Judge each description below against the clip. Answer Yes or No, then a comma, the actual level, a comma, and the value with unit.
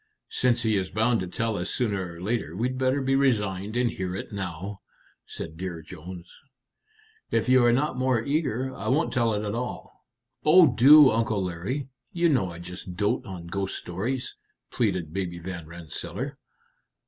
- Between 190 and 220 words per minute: No, average, 170 wpm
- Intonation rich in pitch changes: Yes, wide, 5.8 semitones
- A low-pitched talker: Yes, low, 105 Hz